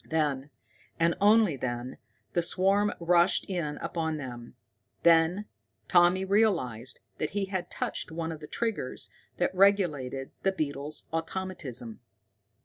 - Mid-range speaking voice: Yes, medium, 165 Hz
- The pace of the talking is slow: Yes, slow, 125 wpm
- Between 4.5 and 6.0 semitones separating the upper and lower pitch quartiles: Yes, average, 5.0 semitones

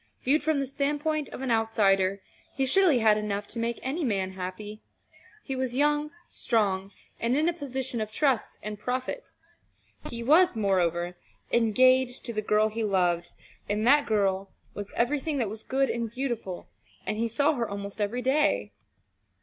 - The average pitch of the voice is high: Yes, high, 230 Hz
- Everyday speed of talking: Yes, average, 165 wpm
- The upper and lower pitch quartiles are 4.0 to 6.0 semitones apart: Yes, average, 4.7 semitones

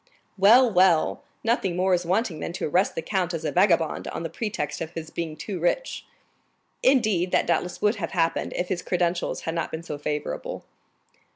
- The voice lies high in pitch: No, medium, 175 Hz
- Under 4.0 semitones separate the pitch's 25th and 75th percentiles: Yes, average, 3.1 semitones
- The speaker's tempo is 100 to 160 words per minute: No, average, 190 wpm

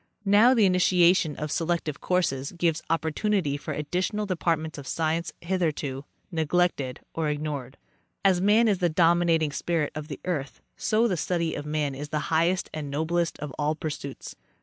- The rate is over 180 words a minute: No, average, 160 wpm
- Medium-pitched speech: Yes, medium, 165 Hz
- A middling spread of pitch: Yes, average, 3.2 semitones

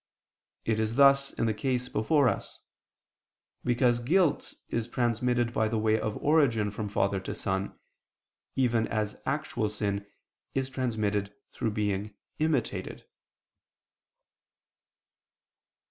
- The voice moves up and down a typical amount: Yes, average, 3.4 semitones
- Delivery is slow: Yes, slow, 115 wpm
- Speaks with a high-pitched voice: No, low, 115 Hz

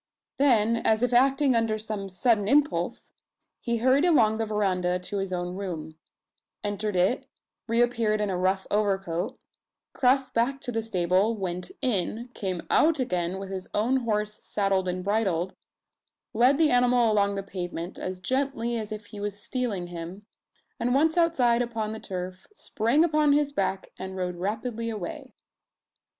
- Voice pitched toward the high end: Yes, high, 215 Hz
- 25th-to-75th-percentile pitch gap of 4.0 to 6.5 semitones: Yes, average, 4.5 semitones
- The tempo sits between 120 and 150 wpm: No, average, 160 wpm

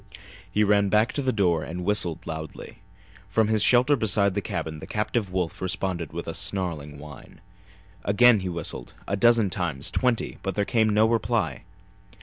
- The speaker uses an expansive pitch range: No, average, 4.1 semitones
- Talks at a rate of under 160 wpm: No, average, 170 wpm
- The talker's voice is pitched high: No, low, 100 Hz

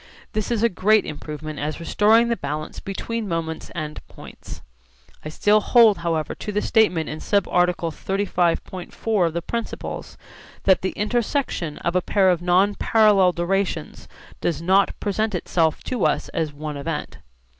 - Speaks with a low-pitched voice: No, medium, 185 Hz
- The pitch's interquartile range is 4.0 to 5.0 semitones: Yes, average, 4.4 semitones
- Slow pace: No, average, 155 wpm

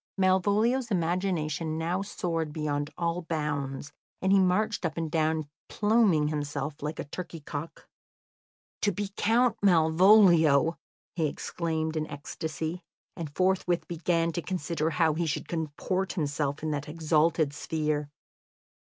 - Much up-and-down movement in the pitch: No, average, 3.2 semitones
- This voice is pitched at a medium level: Yes, medium, 165 Hz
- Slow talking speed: Yes, slow, 130 wpm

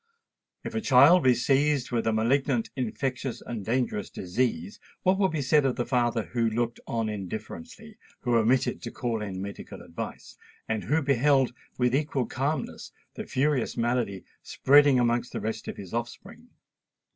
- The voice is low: Yes, low, 125 Hz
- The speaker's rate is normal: Yes, average, 155 wpm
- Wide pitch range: No, average, 3.5 semitones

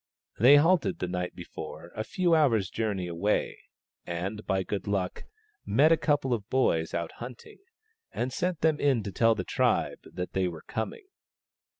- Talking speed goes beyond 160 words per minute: Yes, average, 175 wpm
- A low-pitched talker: Yes, low, 110 Hz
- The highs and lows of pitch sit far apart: Yes, wide, 7.5 semitones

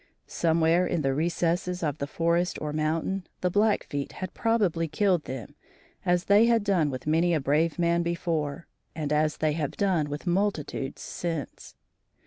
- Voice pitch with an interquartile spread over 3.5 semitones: No, average, 3.0 semitones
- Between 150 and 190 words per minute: Yes, average, 160 wpm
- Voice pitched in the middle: Yes, medium, 165 Hz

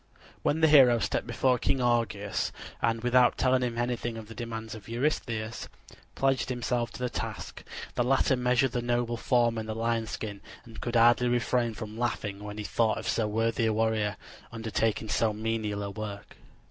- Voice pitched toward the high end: No, low, 115 Hz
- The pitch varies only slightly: Yes, narrow, 1.8 semitones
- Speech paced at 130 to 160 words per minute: No, average, 185 wpm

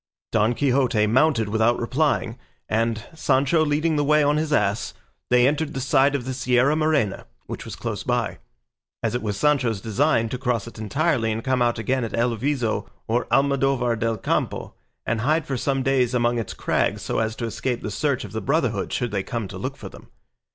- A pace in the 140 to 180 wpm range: No, average, 200 wpm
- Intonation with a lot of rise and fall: No, average, 3.8 semitones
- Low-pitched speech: Yes, low, 125 Hz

